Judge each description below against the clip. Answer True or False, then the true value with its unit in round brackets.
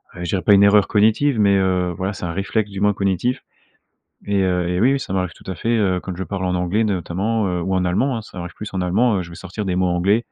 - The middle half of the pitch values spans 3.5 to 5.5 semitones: False (2.6 semitones)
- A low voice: True (95 Hz)